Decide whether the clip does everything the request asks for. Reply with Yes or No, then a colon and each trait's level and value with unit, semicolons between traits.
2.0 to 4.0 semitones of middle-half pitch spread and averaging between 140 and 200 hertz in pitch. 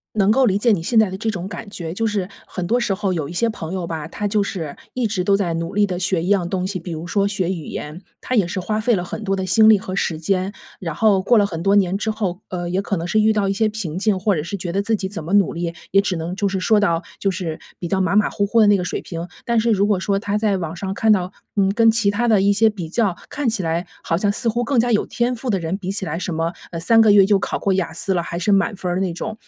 Yes: average, 3.1 semitones; high, 195 Hz